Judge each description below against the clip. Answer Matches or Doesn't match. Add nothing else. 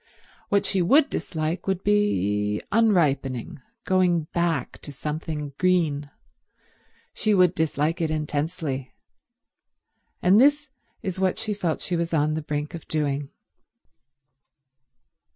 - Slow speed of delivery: Matches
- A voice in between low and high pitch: Matches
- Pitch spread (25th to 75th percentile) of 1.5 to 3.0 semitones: Doesn't match